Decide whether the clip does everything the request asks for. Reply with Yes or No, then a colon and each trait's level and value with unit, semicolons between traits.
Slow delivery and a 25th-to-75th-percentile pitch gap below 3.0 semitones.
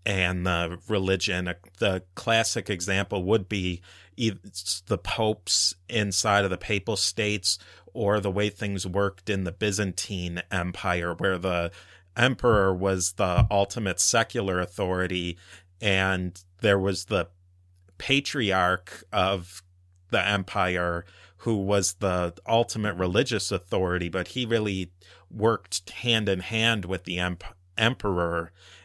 Yes: slow, 120 wpm; narrow, 2.4 semitones